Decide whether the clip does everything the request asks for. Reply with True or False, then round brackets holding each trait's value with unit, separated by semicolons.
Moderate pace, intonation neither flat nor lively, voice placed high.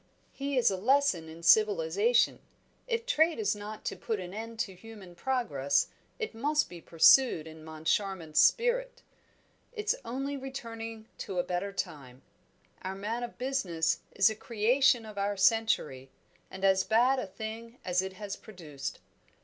False (155 wpm; 5.8 semitones; 215 Hz)